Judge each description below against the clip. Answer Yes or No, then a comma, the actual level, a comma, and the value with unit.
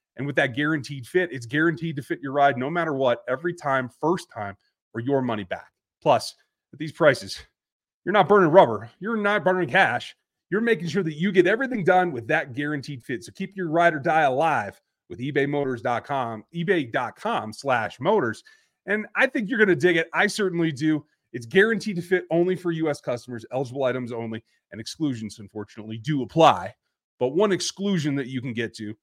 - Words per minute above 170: Yes, average, 185 wpm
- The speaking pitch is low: No, medium, 155 Hz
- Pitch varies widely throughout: Yes, wide, 6.4 semitones